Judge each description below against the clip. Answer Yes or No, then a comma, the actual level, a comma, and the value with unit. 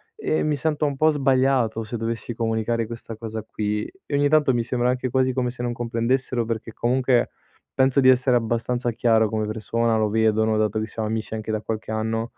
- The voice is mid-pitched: No, low, 115 Hz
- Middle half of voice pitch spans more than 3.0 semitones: No, narrow, 2.6 semitones